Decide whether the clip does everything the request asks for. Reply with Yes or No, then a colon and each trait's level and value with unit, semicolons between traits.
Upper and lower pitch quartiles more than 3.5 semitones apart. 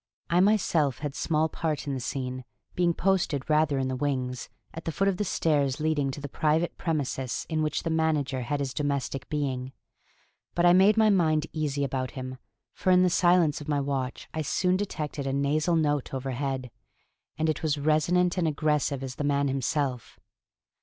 No: average, 3.1 semitones